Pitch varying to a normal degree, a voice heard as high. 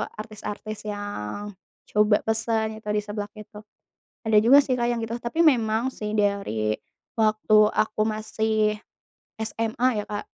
No: narrow, 1.1 semitones; high, 215 Hz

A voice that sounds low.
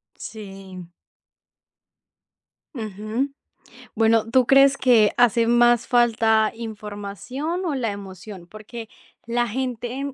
No: high, 230 Hz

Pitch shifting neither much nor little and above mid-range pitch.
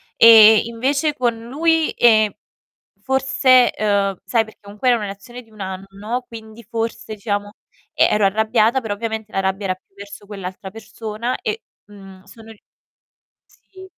Yes: average, 3.0 semitones; high, 220 Hz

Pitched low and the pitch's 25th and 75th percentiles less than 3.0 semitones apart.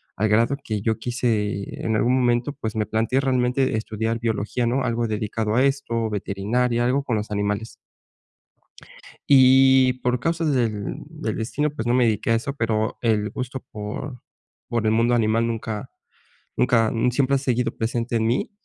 Yes: low, 115 Hz; narrow, 2.6 semitones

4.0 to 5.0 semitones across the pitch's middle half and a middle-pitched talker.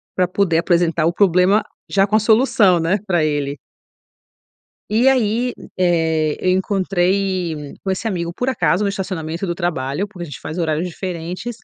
No: average, 3.3 semitones; medium, 180 Hz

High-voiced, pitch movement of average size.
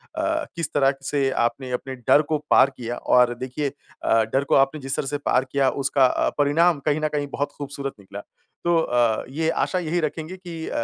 No: medium, 140 Hz; average, 3.0 semitones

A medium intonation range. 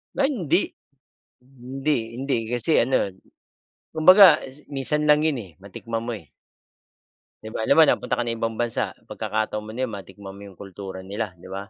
No: wide, 5.9 semitones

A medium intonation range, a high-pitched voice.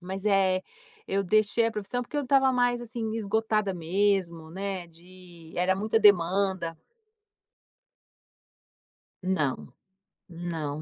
Yes: average, 3.8 semitones; high, 195 Hz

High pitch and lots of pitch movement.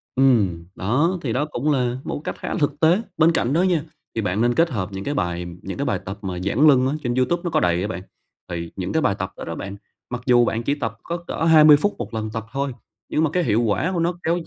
No: low, 125 Hz; wide, 7.5 semitones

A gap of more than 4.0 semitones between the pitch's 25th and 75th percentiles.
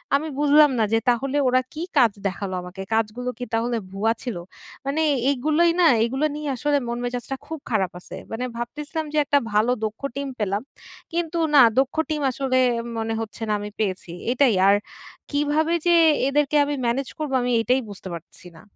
Yes: average, 4.8 semitones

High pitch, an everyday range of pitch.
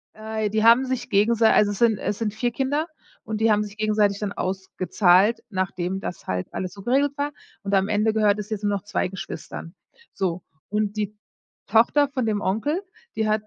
No: high, 210 Hz; narrow, 2.3 semitones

